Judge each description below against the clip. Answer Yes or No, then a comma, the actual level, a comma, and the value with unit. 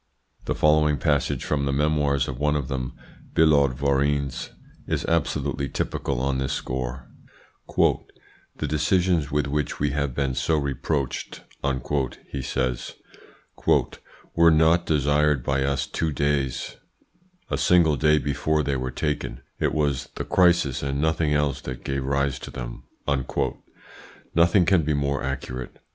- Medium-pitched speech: No, very low, 70 Hz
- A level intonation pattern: Yes, narrow, 2.1 semitones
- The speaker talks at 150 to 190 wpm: No, average, 140 wpm